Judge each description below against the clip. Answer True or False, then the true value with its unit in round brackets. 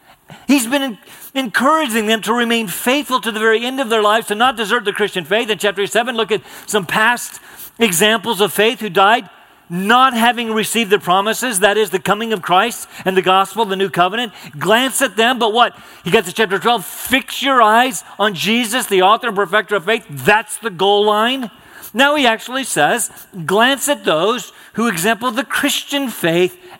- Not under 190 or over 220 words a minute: True (195 wpm)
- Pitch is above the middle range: True (225 Hz)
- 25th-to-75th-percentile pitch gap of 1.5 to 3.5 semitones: True (2.9 semitones)